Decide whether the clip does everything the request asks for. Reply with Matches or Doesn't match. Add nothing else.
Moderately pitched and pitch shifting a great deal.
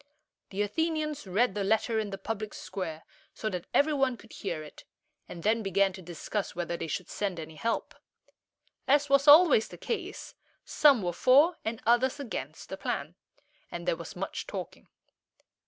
Doesn't match